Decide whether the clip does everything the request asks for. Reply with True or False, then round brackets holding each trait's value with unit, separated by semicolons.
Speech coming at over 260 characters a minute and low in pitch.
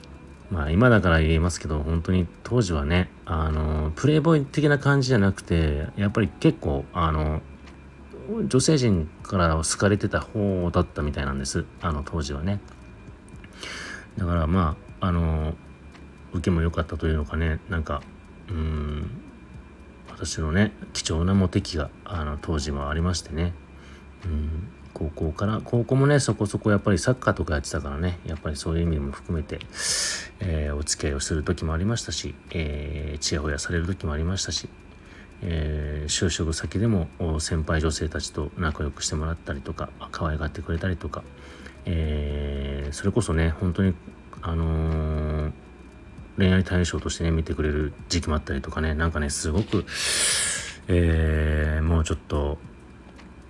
True (320 characters per minute; 80 Hz)